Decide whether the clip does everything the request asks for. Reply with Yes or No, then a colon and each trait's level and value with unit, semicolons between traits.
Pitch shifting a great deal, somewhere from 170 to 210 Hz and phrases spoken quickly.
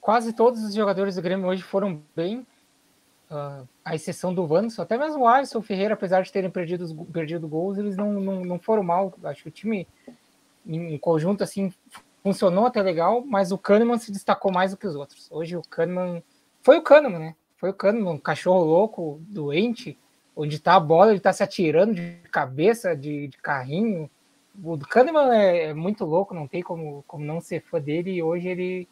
No: average, 3.7 semitones; medium, 185 Hz; fast, 200 wpm